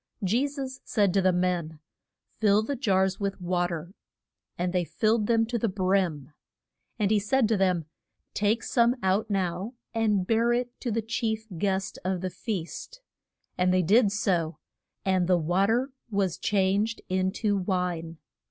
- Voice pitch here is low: No, high, 195 Hz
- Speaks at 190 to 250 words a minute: No, average, 165 wpm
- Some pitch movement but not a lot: Yes, average, 3.6 semitones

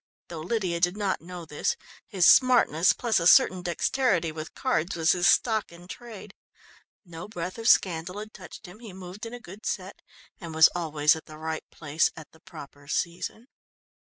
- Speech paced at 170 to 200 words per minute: Yes, average, 185 wpm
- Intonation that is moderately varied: Yes, average, 4.3 semitones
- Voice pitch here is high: No, medium, 175 Hz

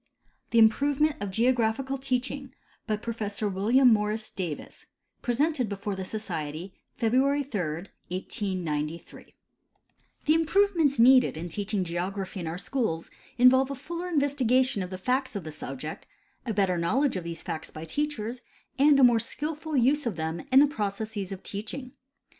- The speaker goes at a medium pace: Yes, average, 150 wpm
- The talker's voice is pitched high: Yes, high, 220 Hz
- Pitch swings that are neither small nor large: No, wide, 6.4 semitones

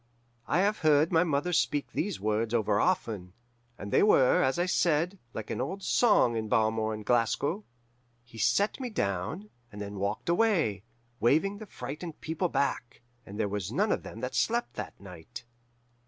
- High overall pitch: No, low, 135 Hz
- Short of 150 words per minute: No, average, 175 wpm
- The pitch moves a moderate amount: No, wide, 8.8 semitones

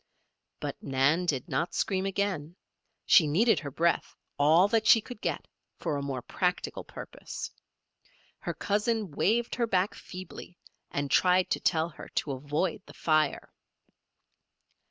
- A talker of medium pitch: Yes, medium, 175 Hz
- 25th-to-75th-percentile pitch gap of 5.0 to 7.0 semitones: Yes, wide, 5.5 semitones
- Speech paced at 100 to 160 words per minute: Yes, average, 140 wpm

